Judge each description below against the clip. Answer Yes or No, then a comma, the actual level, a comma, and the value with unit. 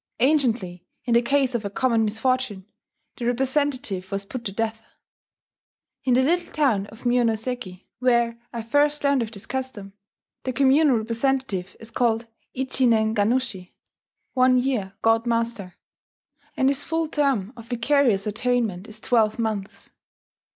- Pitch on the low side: No, high, 235 Hz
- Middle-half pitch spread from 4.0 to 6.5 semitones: No, average, 3.3 semitones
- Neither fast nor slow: Yes, average, 145 wpm